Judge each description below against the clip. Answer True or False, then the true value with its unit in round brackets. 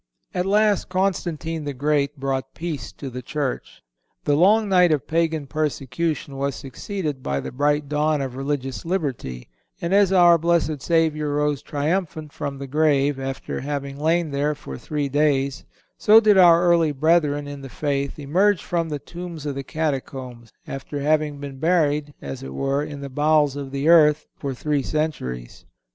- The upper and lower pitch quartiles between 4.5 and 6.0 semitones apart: False (3.0 semitones)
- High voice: False (150 Hz)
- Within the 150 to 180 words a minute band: True (170 wpm)